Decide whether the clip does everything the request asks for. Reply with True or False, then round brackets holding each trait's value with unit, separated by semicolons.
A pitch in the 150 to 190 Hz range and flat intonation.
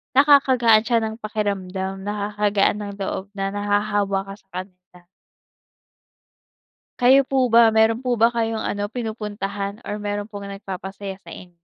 False (205 Hz; 2.3 semitones)